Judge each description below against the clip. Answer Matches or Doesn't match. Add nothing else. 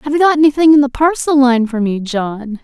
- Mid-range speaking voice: Doesn't match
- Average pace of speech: Doesn't match